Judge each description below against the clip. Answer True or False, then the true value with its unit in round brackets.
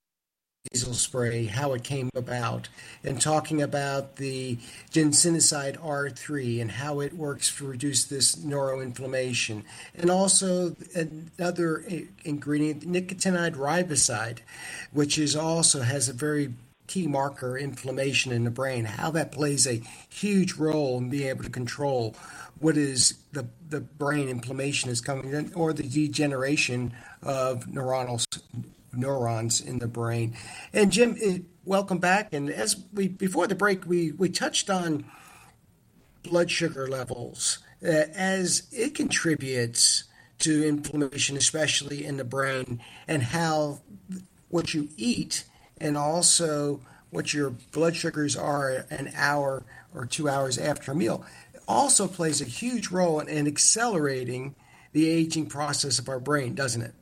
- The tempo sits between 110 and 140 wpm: True (135 wpm)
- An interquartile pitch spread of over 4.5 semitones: False (3.8 semitones)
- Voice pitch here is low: False (145 Hz)